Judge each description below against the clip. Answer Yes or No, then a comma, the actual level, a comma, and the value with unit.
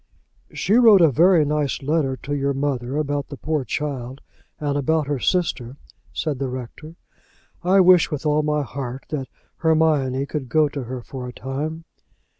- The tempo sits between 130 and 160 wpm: No, average, 170 wpm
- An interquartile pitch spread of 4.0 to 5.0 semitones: No, average, 2.9 semitones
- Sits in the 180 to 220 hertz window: No, medium, 145 Hz